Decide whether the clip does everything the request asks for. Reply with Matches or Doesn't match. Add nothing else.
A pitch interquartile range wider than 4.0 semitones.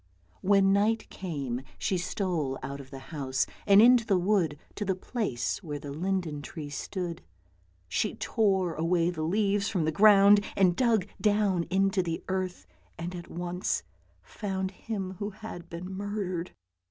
Doesn't match